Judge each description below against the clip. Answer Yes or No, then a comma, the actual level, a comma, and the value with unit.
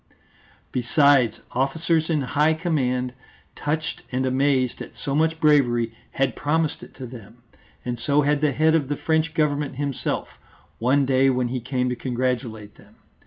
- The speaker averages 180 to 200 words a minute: No, average, 160 wpm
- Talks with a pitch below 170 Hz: Yes, low, 135 Hz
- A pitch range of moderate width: Yes, average, 3.2 semitones